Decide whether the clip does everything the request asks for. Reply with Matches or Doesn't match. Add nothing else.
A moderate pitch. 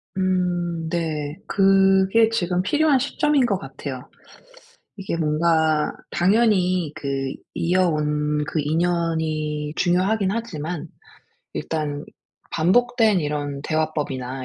Matches